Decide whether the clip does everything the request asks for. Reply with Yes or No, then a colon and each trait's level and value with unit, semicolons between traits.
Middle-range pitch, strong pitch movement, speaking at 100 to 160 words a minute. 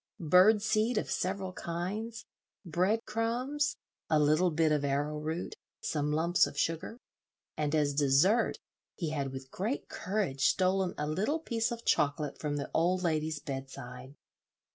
Yes: medium, 165 Hz; wide, 6.0 semitones; average, 140 wpm